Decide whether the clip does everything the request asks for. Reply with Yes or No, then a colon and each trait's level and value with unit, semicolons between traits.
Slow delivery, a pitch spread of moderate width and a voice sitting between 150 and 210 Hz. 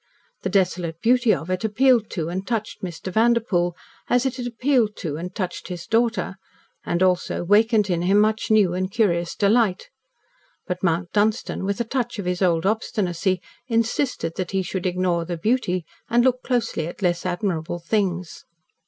No: average, 170 wpm; average, 4.2 semitones; high, 190 Hz